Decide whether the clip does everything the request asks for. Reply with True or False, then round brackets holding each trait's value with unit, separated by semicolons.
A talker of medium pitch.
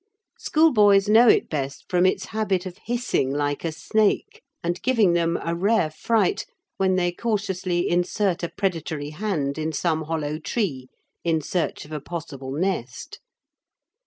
True (175 Hz)